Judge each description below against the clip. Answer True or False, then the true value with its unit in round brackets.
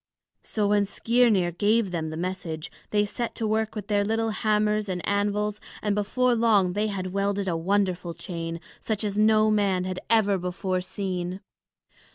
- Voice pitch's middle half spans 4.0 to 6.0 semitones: False (2.6 semitones)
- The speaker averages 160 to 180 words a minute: True (170 wpm)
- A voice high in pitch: True (205 Hz)